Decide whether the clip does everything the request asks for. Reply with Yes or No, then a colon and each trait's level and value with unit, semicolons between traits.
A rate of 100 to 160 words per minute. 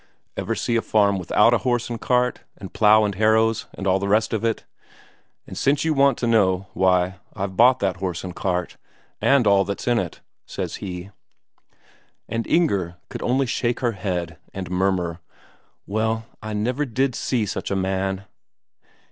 No: average, 175 wpm